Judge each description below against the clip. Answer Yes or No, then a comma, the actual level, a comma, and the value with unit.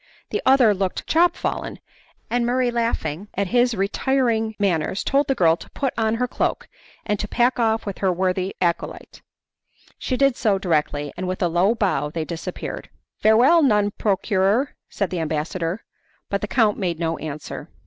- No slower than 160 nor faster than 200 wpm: Yes, average, 170 wpm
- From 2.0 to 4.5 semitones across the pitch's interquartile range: No, average, 5.0 semitones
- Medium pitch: No, high, 205 Hz